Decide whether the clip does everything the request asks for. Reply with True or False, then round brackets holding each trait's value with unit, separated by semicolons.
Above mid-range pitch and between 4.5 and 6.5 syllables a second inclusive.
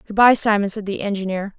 True (205 Hz; 6.4 syllables/s)